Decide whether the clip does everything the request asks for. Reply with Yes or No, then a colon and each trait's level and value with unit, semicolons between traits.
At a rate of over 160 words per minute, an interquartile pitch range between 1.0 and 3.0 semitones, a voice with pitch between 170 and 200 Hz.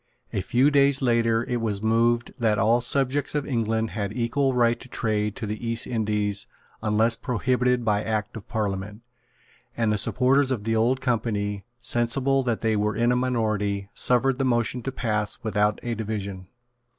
No: average, 175 wpm; average, 2.7 semitones; low, 115 Hz